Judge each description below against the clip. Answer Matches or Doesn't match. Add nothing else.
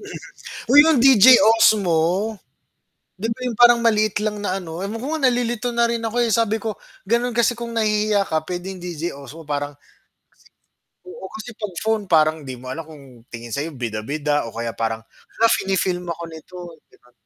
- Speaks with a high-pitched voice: Matches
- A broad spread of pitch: Matches